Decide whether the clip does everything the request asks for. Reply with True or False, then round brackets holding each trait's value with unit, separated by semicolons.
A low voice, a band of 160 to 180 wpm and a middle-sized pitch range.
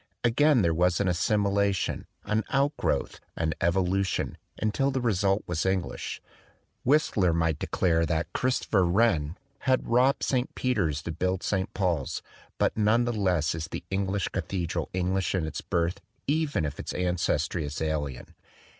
False (95 Hz; 145 wpm; 4.7 semitones)